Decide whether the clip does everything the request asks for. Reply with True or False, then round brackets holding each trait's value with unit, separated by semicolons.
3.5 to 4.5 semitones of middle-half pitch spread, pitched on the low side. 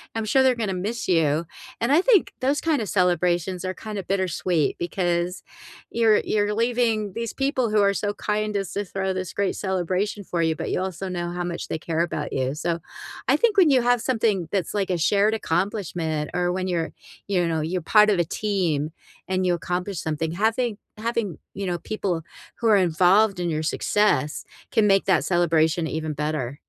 False (3.8 semitones; 185 Hz)